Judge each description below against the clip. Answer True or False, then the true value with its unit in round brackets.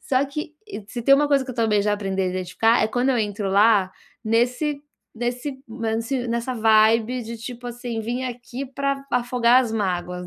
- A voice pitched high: True (235 Hz)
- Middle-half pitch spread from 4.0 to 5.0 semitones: False (2.7 semitones)